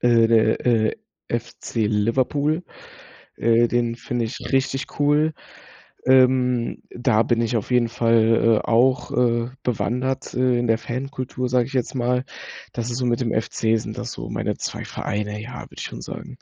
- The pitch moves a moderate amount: No, narrow, 1.9 semitones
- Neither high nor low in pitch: No, low, 120 Hz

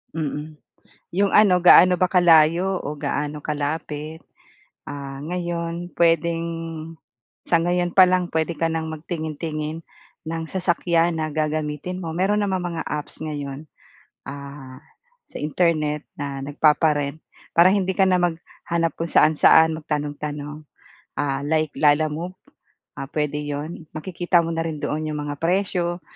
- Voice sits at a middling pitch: Yes, medium, 160 Hz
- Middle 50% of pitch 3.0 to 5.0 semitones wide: No, narrow, 2.6 semitones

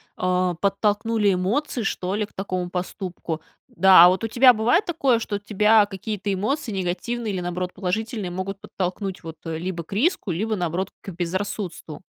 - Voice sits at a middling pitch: No, high, 195 Hz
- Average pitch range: Yes, average, 3.3 semitones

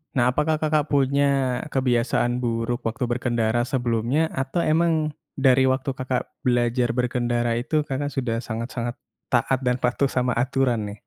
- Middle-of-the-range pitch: No, low, 125 Hz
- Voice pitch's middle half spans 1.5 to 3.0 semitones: Yes, narrow, 2.4 semitones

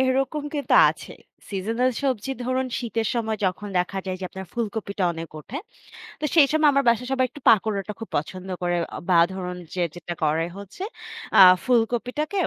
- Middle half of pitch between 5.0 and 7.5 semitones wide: Yes, wide, 5.5 semitones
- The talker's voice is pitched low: No, high, 220 Hz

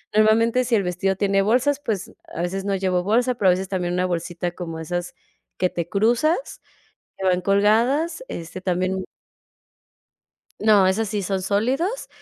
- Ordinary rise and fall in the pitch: Yes, average, 3.8 semitones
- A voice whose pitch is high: Yes, high, 195 Hz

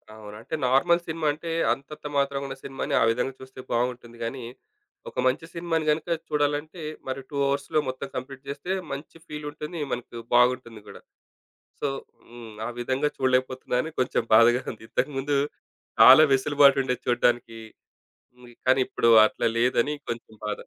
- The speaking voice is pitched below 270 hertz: Yes, low, 135 Hz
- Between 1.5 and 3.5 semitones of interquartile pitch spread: Yes, average, 3.2 semitones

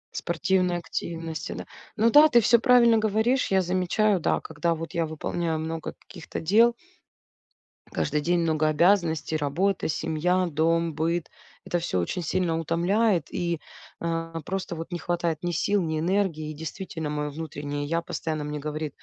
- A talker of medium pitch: Yes, medium, 165 Hz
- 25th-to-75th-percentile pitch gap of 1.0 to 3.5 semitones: Yes, average, 2.9 semitones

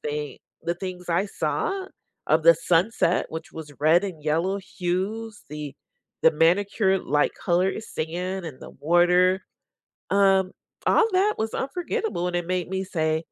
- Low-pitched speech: No, medium, 180 Hz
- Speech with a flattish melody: No, average, 3.1 semitones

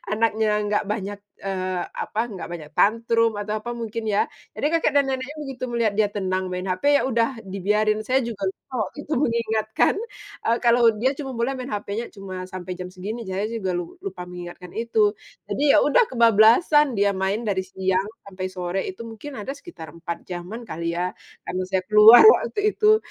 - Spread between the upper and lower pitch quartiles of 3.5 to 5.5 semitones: Yes, average, 3.9 semitones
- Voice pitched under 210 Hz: No, high, 215 Hz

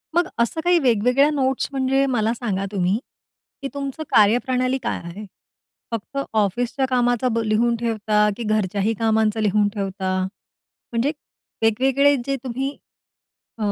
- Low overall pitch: No, high, 235 Hz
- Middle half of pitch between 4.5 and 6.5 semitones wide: No, average, 3.9 semitones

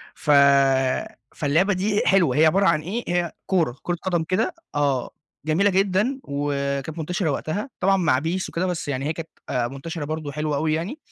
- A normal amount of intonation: Yes, average, 4.3 semitones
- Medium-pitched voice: Yes, medium, 165 Hz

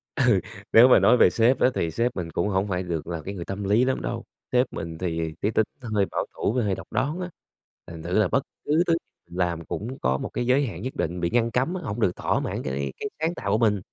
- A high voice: No, low, 105 Hz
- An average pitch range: No, wide, 6.4 semitones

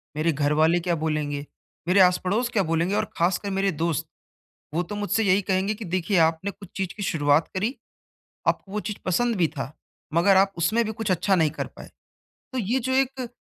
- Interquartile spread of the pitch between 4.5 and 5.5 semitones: No, average, 4.1 semitones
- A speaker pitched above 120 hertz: Yes, medium, 185 Hz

